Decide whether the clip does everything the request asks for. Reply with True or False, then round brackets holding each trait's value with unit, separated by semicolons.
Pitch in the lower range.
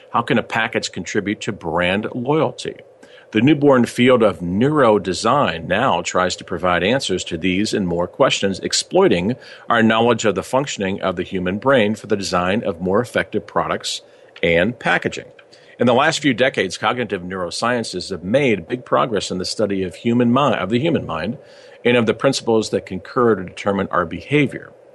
True (110 Hz)